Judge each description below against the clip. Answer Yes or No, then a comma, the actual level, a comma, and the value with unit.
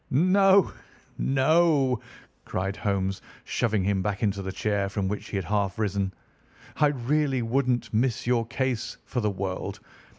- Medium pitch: No, low, 110 Hz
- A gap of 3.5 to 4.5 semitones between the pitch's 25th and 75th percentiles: No, average, 5.1 semitones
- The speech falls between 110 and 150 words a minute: Yes, average, 145 wpm